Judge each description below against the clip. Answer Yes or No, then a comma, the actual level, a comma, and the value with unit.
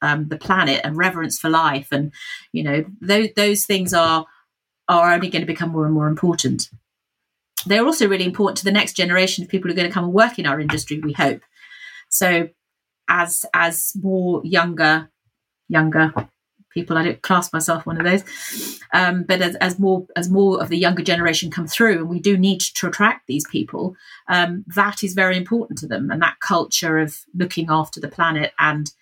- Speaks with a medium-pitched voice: Yes, medium, 175 Hz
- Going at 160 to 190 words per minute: No, average, 200 wpm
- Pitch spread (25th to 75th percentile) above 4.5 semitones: No, average, 3.1 semitones